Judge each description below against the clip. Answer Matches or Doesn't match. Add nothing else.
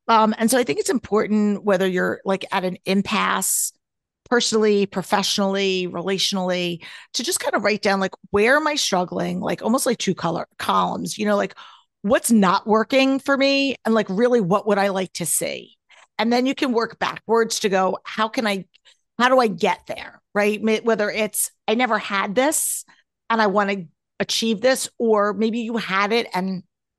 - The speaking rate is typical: Matches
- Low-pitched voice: Doesn't match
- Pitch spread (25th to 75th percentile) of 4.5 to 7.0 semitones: Doesn't match